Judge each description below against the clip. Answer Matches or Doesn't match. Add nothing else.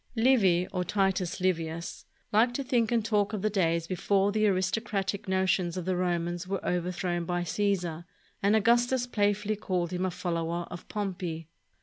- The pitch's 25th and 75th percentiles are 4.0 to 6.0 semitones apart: Doesn't match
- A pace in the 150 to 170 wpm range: Matches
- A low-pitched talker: Doesn't match